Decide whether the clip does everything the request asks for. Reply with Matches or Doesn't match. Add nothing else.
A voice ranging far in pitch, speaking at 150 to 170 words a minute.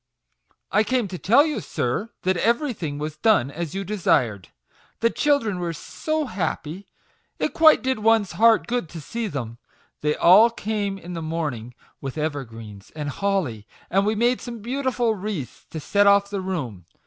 Doesn't match